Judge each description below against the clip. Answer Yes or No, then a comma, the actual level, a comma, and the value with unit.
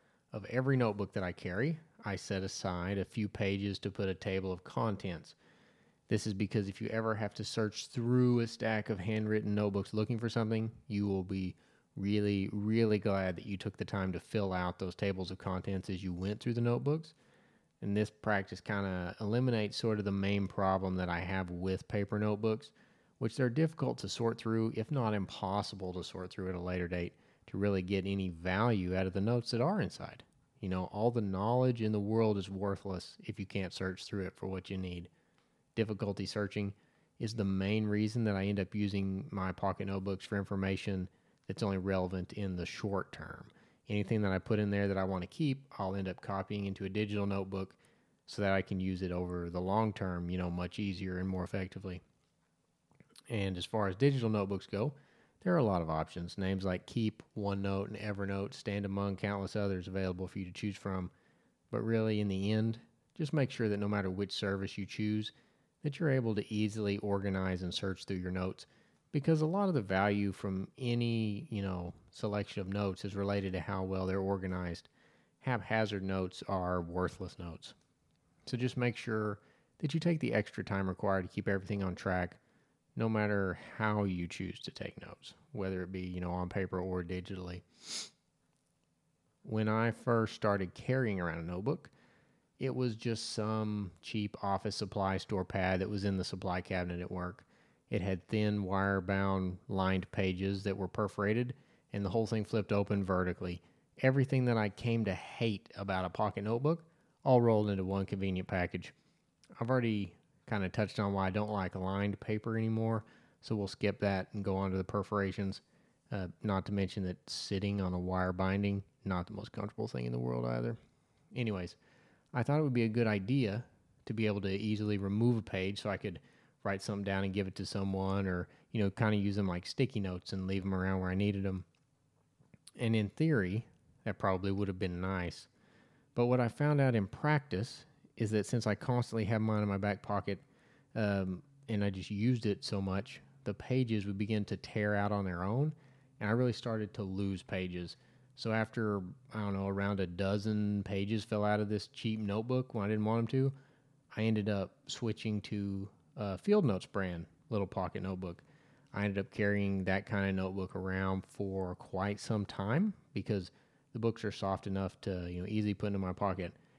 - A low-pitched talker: Yes, low, 100 Hz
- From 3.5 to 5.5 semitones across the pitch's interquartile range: No, average, 2.7 semitones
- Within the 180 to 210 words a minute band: Yes, average, 200 wpm